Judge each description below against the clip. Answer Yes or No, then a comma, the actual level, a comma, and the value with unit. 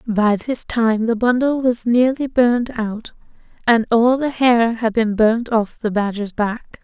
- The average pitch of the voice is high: Yes, high, 230 Hz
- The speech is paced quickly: No, average, 175 wpm